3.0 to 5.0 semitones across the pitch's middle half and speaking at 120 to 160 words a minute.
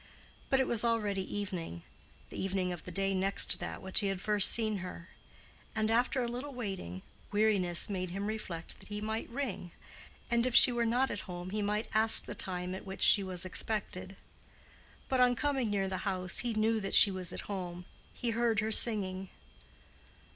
No: average, 3.4 semitones; average, 190 wpm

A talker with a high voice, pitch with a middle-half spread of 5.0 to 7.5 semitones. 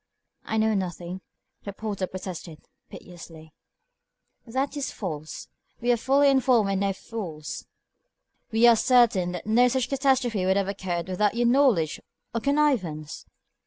Yes: high, 205 Hz; wide, 5.4 semitones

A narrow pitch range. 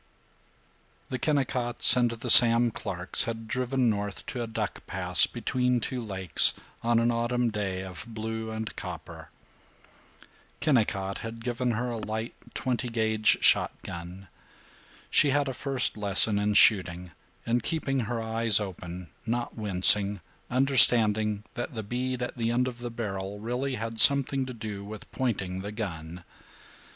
No: average, 3.1 semitones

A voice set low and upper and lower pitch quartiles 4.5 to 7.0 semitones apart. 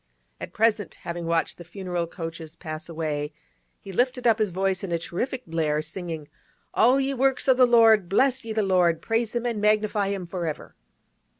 No: high, 195 Hz; average, 5.3 semitones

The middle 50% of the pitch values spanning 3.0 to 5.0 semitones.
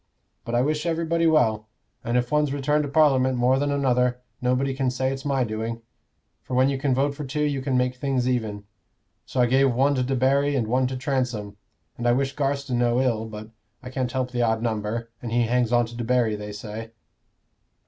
No: narrow, 2.6 semitones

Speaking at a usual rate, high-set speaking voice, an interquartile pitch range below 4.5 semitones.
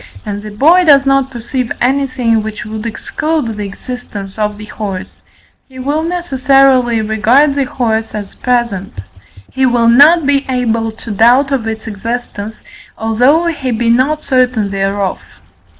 Yes: average, 150 wpm; high, 240 Hz; average, 4.0 semitones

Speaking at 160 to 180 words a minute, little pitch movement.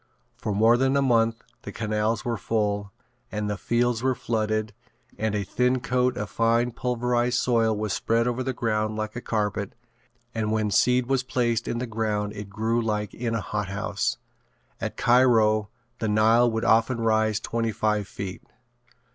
Yes: average, 170 wpm; narrow, 2.2 semitones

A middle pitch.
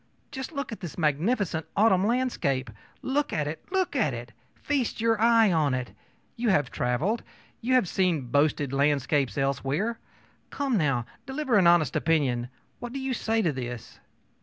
Yes: medium, 175 Hz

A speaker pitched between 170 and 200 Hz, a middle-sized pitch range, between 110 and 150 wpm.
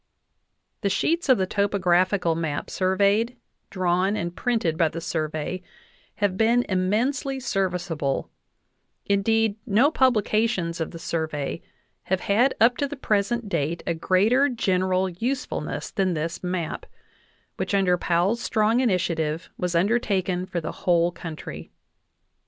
Yes: high, 190 Hz; average, 4.6 semitones; slow, 135 wpm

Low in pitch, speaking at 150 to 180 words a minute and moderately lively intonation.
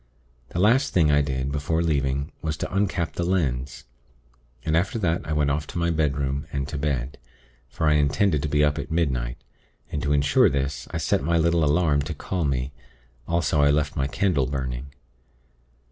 No: very low, 75 Hz; average, 190 wpm; average, 3.1 semitones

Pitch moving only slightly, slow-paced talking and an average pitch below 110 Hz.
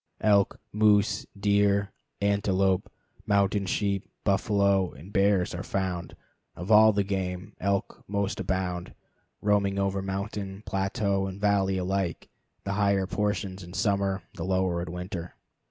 Yes: narrow, 1.3 semitones; slow, 130 wpm; low, 100 Hz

